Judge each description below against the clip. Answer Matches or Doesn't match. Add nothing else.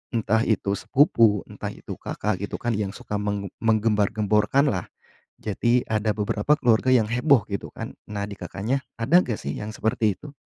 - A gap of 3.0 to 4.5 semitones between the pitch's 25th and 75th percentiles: Doesn't match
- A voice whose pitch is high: Doesn't match